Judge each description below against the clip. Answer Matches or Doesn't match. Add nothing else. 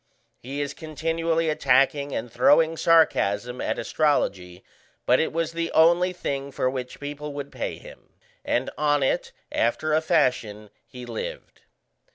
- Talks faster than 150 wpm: Doesn't match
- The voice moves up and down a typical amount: Matches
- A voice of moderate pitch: Matches